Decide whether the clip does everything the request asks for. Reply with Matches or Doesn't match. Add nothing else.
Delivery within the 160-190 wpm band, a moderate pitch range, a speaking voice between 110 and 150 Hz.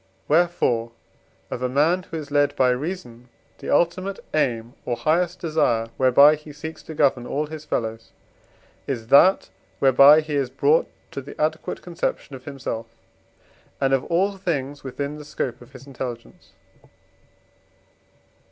Doesn't match